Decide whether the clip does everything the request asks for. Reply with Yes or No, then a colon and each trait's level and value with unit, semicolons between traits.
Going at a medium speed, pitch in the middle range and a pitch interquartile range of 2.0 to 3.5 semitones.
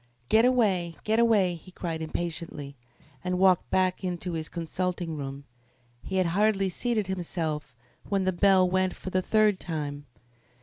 Yes: average, 155 wpm; medium, 180 Hz; average, 2.7 semitones